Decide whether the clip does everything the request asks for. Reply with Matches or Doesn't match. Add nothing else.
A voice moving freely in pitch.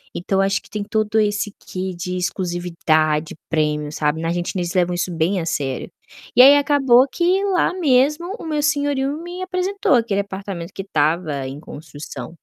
Matches